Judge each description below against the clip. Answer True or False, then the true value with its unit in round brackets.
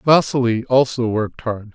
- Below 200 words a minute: True (140 wpm)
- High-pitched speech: False (120 Hz)